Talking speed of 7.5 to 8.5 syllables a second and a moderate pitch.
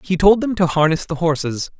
No: 5.5 syllables/s; medium, 170 Hz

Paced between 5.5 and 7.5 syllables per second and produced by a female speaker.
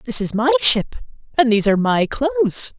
Yes: 6.9 syllables/s; female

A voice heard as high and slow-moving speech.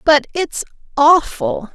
Yes: very high, 280 Hz; slow, 105 wpm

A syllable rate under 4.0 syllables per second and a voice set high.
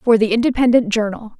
No: 6.0 syllables/s; high, 225 Hz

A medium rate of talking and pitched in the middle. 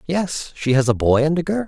No: fast, 285 wpm; medium, 155 Hz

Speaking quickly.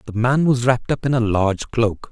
Yes: fast, 255 wpm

